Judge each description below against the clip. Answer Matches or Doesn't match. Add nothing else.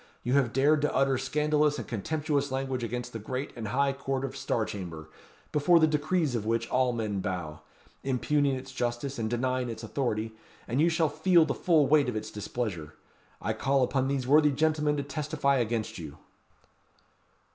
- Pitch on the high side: Doesn't match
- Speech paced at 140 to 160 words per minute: Doesn't match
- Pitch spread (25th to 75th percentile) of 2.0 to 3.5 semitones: Doesn't match